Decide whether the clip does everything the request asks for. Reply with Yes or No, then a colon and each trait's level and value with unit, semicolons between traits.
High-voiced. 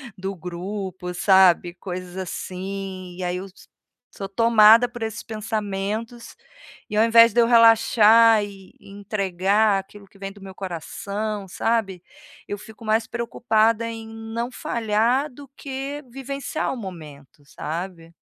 Yes: high, 205 Hz